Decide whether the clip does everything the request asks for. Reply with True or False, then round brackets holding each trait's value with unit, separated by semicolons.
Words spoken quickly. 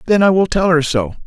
True (285 wpm)